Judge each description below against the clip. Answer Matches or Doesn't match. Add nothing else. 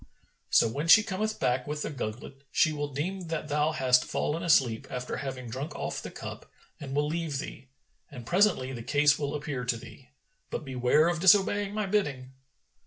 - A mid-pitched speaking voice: Matches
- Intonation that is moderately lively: Matches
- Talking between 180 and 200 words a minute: Matches